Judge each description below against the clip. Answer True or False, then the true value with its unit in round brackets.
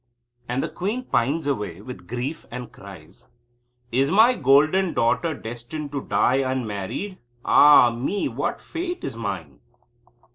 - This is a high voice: False (135 Hz)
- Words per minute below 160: True (140 wpm)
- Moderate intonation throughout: False (5.9 semitones)